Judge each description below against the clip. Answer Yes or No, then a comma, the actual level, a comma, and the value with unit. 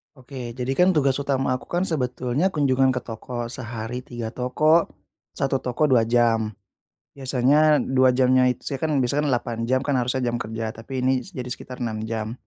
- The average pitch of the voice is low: Yes, low, 125 Hz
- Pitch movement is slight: Yes, narrow, 2.2 semitones